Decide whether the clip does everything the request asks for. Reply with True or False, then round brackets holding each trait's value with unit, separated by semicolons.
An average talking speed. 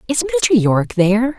True (175 wpm)